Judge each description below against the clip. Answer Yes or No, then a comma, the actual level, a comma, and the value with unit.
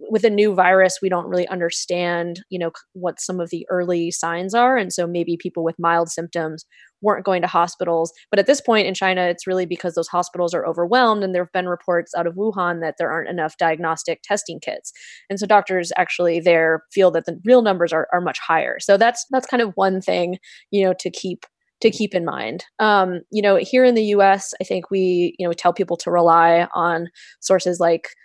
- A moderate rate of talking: No, fast, 220 wpm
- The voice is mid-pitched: Yes, medium, 180 Hz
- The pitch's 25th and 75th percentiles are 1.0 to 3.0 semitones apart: Yes, narrow, 2.5 semitones